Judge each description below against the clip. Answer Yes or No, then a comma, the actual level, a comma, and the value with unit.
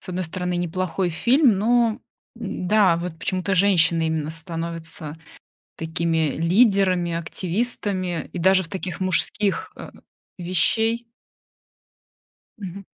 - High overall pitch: No, medium, 180 Hz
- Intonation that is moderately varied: Yes, average, 3.1 semitones